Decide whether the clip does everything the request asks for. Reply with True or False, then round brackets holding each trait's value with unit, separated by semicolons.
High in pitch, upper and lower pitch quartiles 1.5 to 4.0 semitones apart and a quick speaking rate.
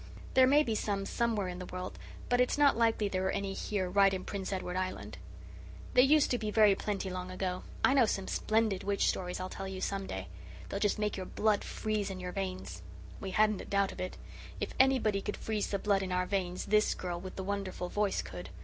True (195 Hz; 2.4 semitones; 230 wpm)